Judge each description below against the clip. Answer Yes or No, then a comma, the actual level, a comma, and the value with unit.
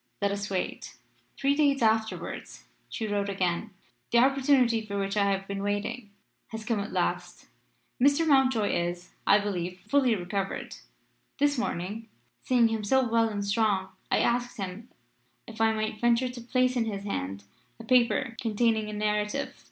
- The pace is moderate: Yes, average, 160 wpm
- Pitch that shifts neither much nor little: Yes, average, 3.4 semitones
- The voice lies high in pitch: Yes, high, 220 Hz